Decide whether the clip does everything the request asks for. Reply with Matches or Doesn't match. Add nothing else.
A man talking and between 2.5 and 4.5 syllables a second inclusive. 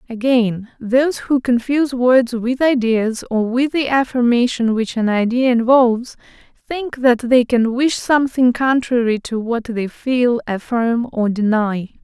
Doesn't match